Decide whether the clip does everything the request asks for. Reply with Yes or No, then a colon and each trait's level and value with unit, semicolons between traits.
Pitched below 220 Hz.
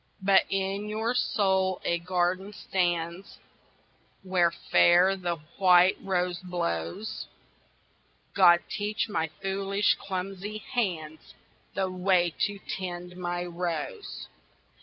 Yes: medium, 185 Hz